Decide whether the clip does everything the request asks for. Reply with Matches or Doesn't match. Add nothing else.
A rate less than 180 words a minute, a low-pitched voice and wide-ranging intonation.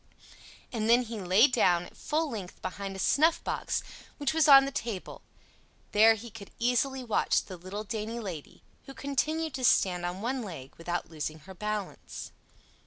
Doesn't match